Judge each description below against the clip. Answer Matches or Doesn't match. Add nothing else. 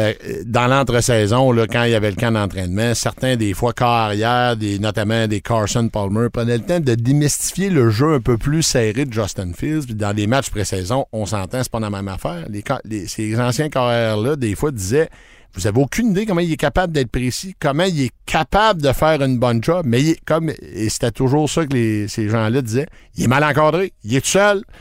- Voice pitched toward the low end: Matches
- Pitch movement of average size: Matches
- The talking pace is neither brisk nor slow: Doesn't match